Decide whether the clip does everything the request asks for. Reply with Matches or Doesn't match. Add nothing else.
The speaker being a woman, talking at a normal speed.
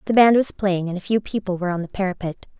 Doesn't match